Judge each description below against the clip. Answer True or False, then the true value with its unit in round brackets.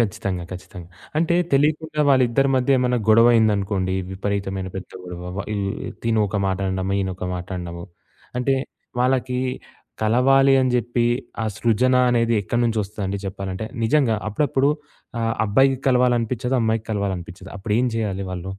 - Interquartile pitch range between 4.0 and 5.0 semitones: True (4.7 semitones)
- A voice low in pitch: True (110 Hz)